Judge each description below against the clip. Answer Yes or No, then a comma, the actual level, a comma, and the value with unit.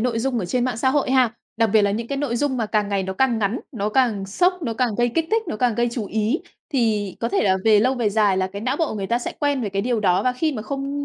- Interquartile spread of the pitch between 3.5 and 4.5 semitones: Yes, average, 3.9 semitones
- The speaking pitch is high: Yes, high, 235 Hz